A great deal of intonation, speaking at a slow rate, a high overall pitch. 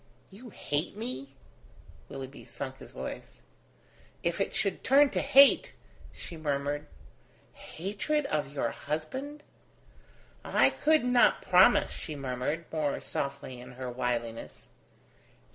No: wide, 8.7 semitones; slow, 115 wpm; medium, 150 Hz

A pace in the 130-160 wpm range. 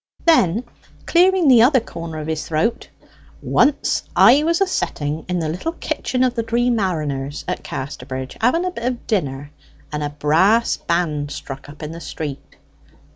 No: average, 170 wpm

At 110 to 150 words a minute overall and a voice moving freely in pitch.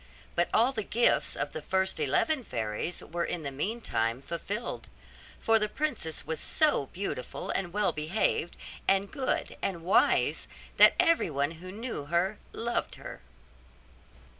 Yes: average, 140 wpm; wide, 6.0 semitones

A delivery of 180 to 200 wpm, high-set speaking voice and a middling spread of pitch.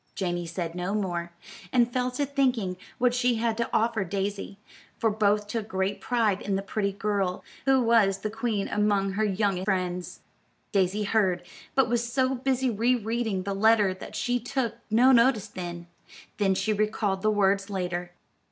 No: average, 170 wpm; high, 210 Hz; average, 3.4 semitones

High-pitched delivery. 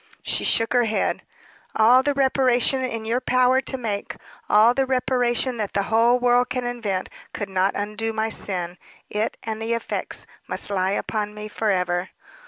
Yes: high, 225 Hz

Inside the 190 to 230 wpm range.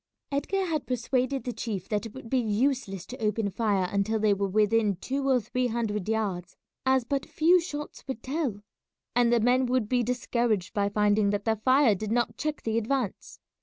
Yes: average, 195 wpm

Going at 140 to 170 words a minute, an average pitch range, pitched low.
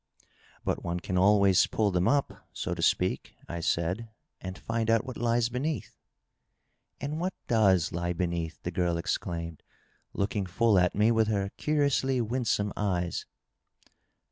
Yes: average, 165 wpm; average, 4.8 semitones; low, 100 Hz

